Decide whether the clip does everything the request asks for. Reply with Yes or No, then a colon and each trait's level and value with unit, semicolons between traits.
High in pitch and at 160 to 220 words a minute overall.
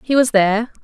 Yes: high, 225 Hz; fast, 215 wpm